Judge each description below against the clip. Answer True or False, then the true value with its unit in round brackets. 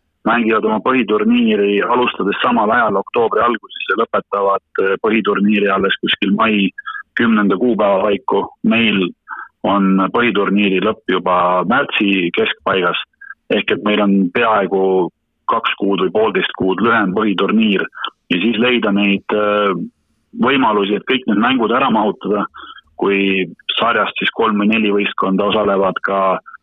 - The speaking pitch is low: True (100 Hz)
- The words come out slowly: True (125 wpm)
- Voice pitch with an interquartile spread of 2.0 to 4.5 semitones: True (2.7 semitones)